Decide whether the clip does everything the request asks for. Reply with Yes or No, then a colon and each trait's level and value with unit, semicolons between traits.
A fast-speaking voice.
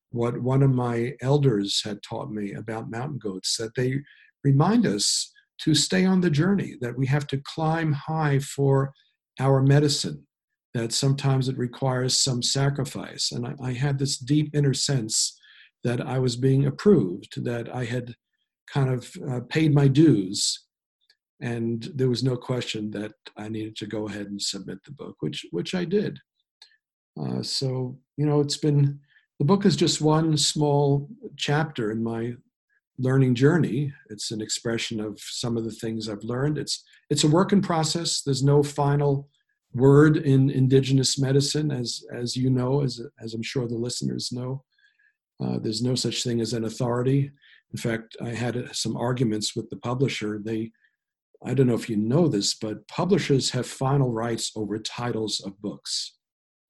No: average, 170 wpm